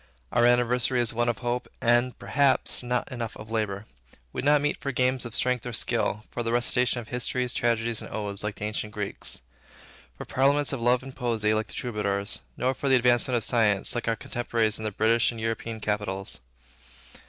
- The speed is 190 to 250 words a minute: Yes, average, 200 wpm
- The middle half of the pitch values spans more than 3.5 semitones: No, narrow, 2.5 semitones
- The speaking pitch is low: Yes, low, 120 Hz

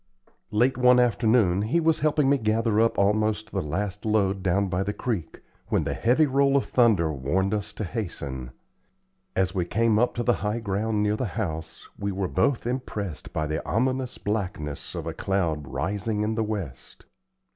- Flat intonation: No, average, 3.9 semitones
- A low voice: Yes, low, 105 Hz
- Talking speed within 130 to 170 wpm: No, average, 180 wpm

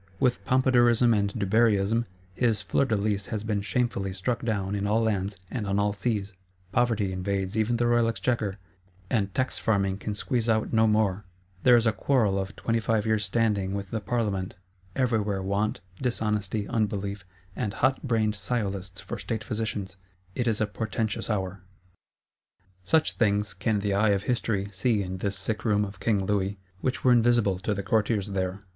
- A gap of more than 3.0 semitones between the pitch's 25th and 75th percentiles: No, narrow, 2.5 semitones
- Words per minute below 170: No, average, 175 wpm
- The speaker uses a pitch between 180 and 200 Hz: No, low, 105 Hz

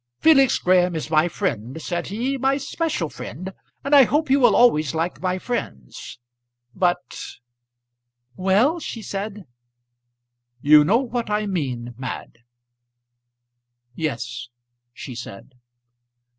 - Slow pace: Yes, slow, 120 wpm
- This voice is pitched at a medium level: Yes, medium, 180 Hz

